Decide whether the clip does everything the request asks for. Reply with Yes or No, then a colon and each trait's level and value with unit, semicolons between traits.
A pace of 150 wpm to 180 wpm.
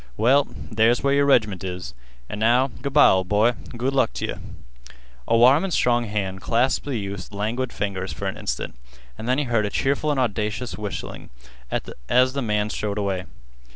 No: average, 190 wpm